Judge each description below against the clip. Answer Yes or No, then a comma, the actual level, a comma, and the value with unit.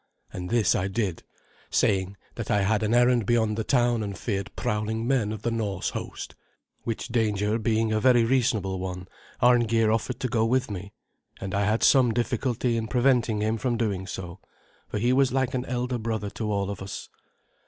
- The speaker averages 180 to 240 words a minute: Yes, average, 190 wpm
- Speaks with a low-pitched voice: Yes, low, 110 Hz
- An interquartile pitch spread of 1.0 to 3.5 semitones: Yes, average, 3.1 semitones